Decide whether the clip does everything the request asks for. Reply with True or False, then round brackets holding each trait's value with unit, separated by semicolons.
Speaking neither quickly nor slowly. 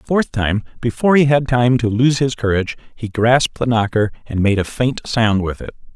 False (220 wpm)